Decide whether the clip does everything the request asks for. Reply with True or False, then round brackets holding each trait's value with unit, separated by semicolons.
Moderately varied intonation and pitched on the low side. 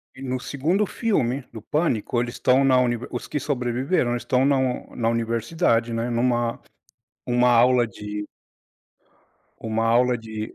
False (2.2 semitones; 120 Hz)